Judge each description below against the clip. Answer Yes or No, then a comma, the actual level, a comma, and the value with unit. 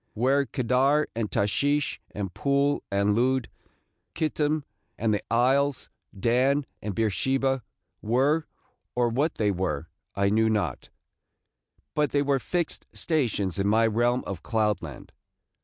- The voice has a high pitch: No, low, 120 Hz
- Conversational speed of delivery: No, slow, 130 wpm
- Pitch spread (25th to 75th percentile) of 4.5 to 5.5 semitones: Yes, average, 5.1 semitones